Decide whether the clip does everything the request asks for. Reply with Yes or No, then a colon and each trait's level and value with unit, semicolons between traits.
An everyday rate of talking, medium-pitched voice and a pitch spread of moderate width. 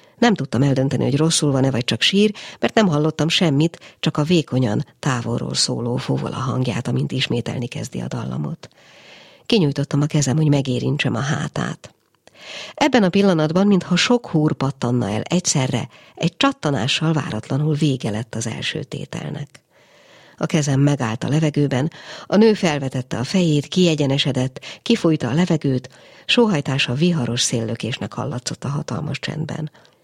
Yes: average, 140 wpm; medium, 145 Hz; average, 4.2 semitones